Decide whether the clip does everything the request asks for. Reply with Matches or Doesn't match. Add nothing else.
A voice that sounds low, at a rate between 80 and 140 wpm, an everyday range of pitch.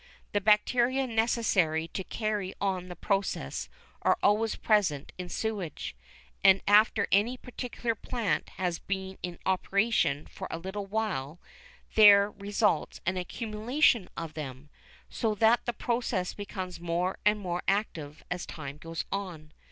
Doesn't match